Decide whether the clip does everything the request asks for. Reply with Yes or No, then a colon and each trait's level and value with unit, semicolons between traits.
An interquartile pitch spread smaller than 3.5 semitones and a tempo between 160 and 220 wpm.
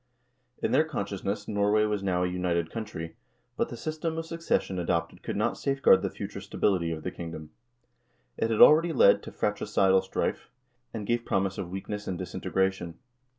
No: average, 4.0 semitones; average, 170 wpm